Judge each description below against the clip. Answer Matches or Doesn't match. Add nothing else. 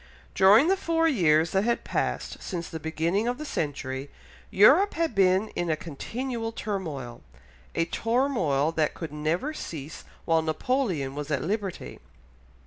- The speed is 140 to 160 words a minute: Matches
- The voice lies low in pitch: Doesn't match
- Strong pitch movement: Matches